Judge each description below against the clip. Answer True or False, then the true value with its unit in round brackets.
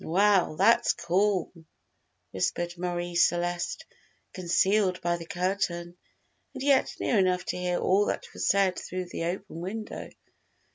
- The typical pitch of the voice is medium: True (180 Hz)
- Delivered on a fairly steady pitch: True (2.2 semitones)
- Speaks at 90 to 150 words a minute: True (135 wpm)